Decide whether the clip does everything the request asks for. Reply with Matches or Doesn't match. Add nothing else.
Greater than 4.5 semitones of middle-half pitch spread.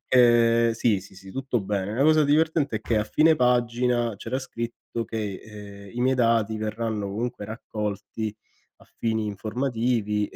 Doesn't match